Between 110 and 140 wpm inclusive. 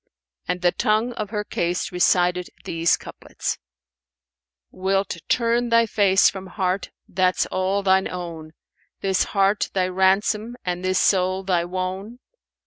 Yes: slow, 135 wpm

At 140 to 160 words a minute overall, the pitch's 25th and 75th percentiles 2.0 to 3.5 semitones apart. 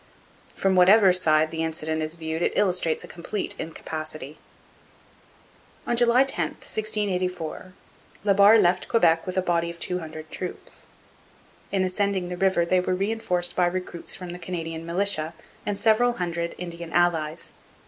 Yes: average, 150 wpm; average, 3.0 semitones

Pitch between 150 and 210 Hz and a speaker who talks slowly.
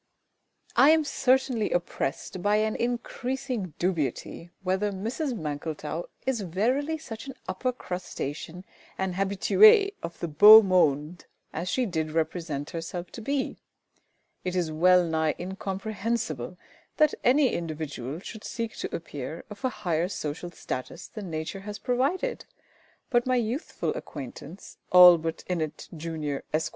Yes: medium, 185 Hz; slow, 130 wpm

